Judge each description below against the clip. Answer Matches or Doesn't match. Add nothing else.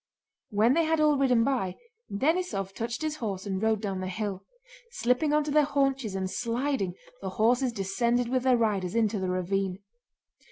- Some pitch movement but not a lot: Doesn't match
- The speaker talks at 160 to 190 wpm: Matches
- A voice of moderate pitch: Doesn't match